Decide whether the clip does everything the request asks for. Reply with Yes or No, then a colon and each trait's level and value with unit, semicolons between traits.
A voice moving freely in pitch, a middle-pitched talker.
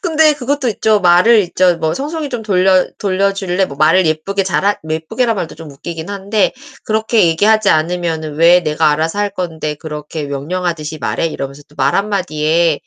No: average, 4.6 semitones; medium, 180 Hz